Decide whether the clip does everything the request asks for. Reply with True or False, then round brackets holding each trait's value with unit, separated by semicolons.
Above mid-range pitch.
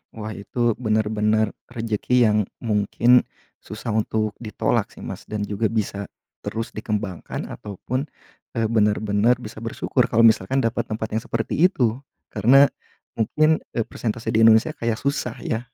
False (110 Hz)